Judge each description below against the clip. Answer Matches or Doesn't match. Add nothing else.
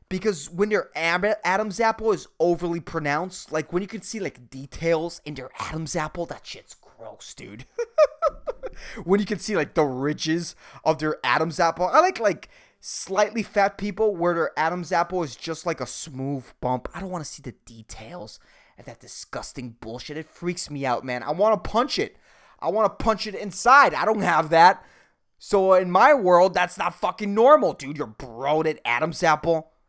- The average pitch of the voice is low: Doesn't match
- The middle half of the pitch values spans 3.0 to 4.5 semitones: Doesn't match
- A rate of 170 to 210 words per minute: Matches